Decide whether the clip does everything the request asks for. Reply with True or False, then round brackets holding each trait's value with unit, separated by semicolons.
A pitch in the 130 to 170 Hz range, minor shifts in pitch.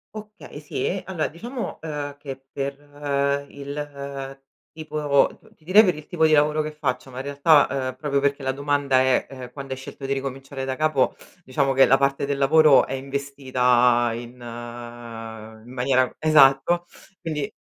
True (140 Hz; 2.2 semitones)